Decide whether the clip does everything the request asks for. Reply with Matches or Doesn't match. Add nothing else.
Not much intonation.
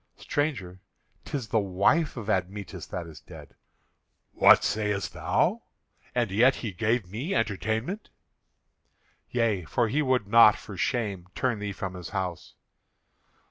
Doesn't match